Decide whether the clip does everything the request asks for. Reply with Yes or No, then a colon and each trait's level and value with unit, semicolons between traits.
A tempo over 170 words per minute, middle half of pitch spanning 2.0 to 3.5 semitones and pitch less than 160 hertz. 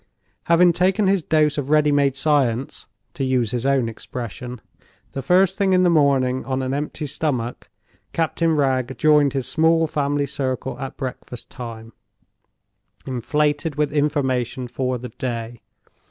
No: average, 145 wpm; average, 3.2 semitones; medium, 140 Hz